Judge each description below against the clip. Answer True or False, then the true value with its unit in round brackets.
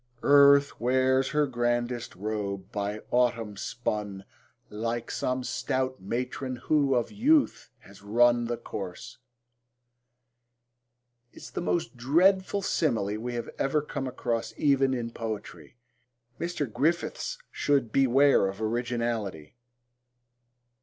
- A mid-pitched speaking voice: False (120 Hz)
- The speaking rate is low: True (110 wpm)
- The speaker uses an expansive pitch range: False (4.0 semitones)